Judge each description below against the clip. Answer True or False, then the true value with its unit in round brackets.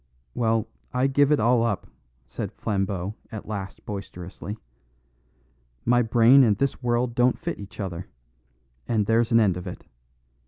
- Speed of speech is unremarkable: True (150 wpm)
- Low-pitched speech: True (110 Hz)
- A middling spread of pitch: True (3.5 semitones)